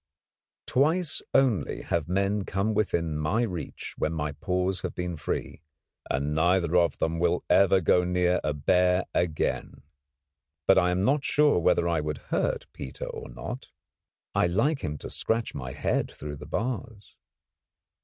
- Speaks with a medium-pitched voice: No, very low, 90 Hz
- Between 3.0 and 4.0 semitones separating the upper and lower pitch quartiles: No, average, 4.5 semitones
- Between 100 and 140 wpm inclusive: No, average, 160 wpm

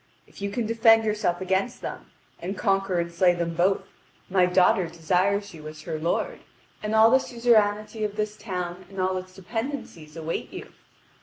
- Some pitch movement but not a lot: Yes, average, 3.4 semitones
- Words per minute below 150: No, average, 170 wpm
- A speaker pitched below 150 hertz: No, high, 190 Hz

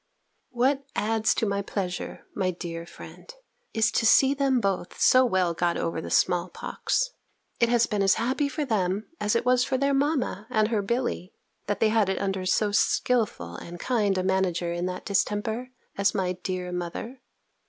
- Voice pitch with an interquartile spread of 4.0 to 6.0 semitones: Yes, average, 5.0 semitones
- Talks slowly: No, average, 185 wpm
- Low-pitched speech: No, high, 205 Hz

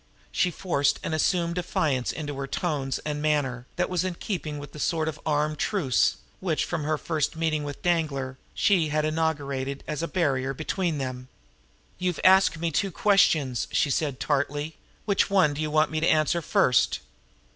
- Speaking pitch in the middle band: Yes, medium, 155 Hz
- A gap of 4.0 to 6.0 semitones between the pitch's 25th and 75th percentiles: No, average, 3.0 semitones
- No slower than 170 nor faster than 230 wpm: Yes, average, 180 wpm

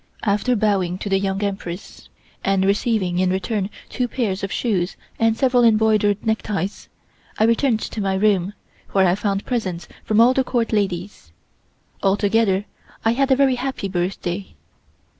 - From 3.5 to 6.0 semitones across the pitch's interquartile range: No, average, 2.9 semitones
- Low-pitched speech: No, high, 205 Hz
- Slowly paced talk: No, average, 155 wpm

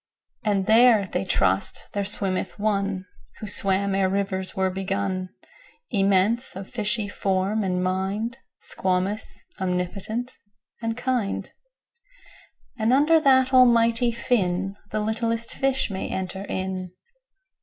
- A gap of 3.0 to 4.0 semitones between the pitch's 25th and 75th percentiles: Yes, average, 3.6 semitones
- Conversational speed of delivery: No, slow, 100 wpm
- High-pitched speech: Yes, high, 200 Hz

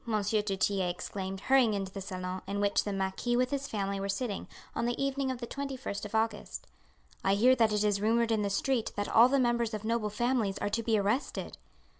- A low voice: No, high, 215 Hz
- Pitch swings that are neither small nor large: Yes, average, 3.3 semitones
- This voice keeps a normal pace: No, fast, 220 wpm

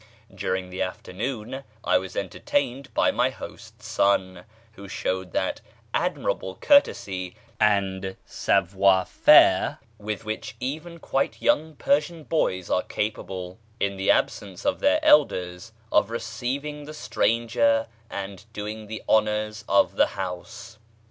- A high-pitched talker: No, low, 105 Hz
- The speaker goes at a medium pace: No, slow, 125 wpm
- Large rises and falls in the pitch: No, average, 4.5 semitones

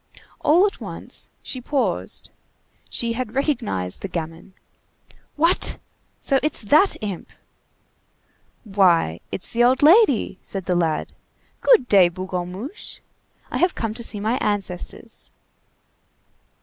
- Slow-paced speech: Yes, slow, 120 wpm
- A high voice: Yes, high, 220 Hz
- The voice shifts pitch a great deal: Yes, wide, 6.8 semitones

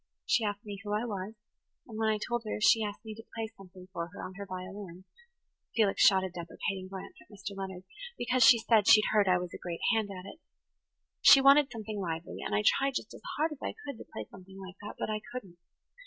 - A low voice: No, high, 205 Hz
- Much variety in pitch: No, average, 3.1 semitones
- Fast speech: Yes, fast, 230 wpm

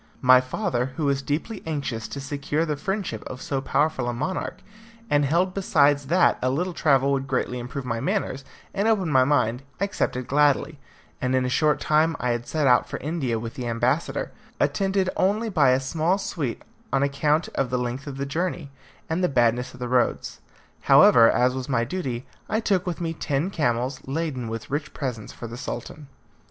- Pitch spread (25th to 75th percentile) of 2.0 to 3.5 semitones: No, average, 4.3 semitones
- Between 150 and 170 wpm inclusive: No, average, 190 wpm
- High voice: No, medium, 140 Hz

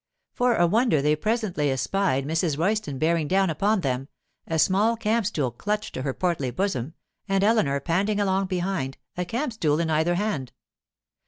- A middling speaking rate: Yes, average, 170 wpm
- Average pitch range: No, wide, 5.7 semitones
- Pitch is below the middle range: No, medium, 175 Hz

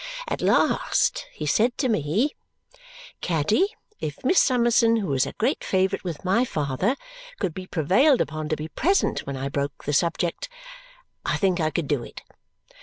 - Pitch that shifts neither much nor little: No, wide, 7.8 semitones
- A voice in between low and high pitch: Yes, medium, 175 Hz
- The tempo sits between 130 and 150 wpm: No, average, 170 wpm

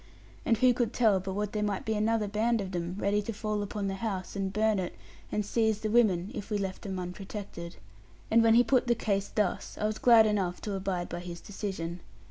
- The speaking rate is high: Yes, fast, 225 wpm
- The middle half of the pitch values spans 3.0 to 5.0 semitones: No, narrow, 2.4 semitones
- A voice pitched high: Yes, high, 205 Hz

